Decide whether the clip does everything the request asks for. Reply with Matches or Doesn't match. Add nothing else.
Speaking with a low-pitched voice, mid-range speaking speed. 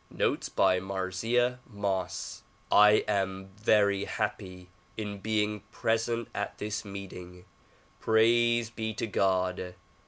Doesn't match